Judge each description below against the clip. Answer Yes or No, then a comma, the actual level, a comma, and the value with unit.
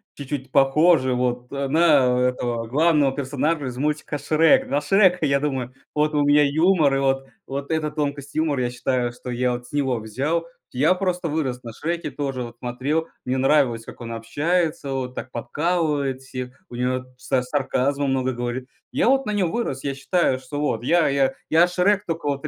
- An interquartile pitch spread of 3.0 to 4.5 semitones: Yes, average, 3.6 semitones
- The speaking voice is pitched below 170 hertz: Yes, medium, 140 Hz